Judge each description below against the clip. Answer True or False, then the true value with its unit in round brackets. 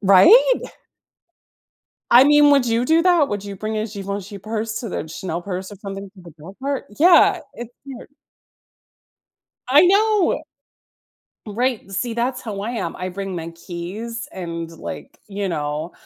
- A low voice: False (210 Hz)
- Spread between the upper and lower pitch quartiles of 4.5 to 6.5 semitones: True (5.5 semitones)